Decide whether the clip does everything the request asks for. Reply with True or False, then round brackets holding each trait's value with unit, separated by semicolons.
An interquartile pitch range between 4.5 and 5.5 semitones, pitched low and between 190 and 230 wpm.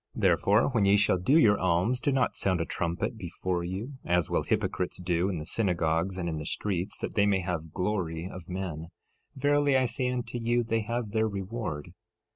True (4.8 semitones; 95 Hz; 205 wpm)